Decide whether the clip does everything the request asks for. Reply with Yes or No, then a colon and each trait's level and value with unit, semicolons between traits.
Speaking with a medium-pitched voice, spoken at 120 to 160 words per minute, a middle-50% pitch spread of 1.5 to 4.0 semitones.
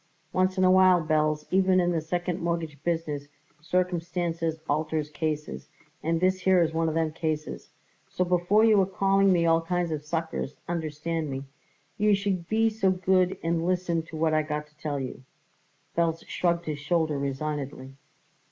No: medium, 165 Hz; average, 170 wpm; average, 2.9 semitones